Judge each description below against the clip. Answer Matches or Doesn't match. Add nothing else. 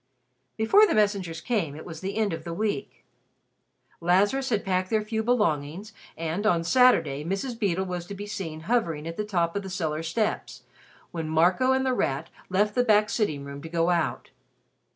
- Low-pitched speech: Doesn't match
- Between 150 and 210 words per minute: Matches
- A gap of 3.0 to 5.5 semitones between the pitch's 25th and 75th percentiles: Matches